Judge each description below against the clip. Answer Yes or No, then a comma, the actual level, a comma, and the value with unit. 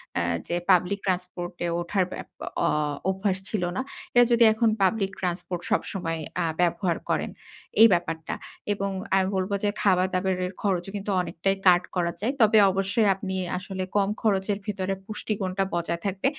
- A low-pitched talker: No, high, 190 Hz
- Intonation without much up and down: Yes, narrow, 2.0 semitones